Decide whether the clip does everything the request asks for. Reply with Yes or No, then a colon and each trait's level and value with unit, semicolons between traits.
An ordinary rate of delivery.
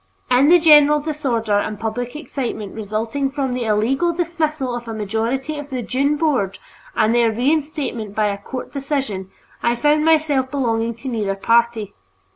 Yes: average, 160 wpm